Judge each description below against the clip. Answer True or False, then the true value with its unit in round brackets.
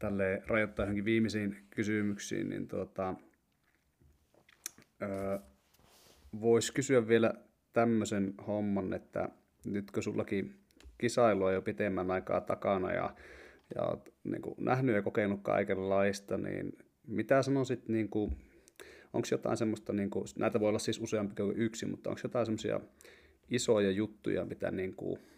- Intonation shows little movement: True (2.3 semitones)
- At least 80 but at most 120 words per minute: False (130 wpm)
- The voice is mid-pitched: False (105 Hz)